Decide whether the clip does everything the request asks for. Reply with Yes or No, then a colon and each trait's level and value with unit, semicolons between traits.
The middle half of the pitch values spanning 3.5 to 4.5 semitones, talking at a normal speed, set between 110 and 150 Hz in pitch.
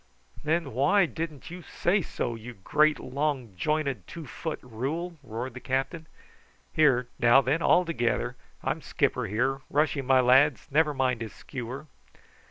Yes: average, 4.0 semitones; average, 155 wpm; low, 135 Hz